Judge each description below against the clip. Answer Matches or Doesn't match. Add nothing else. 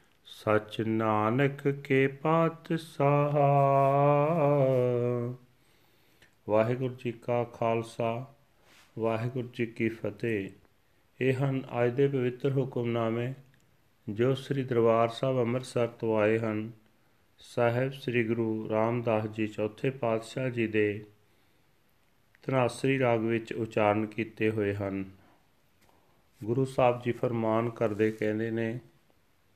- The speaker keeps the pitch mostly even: Doesn't match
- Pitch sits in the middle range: Doesn't match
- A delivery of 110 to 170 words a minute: Doesn't match